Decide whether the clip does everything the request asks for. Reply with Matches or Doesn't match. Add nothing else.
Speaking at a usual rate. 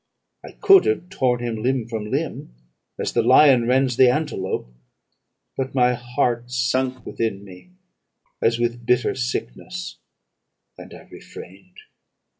Doesn't match